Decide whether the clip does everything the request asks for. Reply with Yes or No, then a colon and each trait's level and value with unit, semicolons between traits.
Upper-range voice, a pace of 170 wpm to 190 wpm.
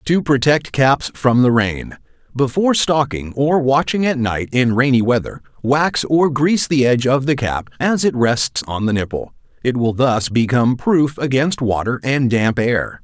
No: low, 130 Hz; average, 175 wpm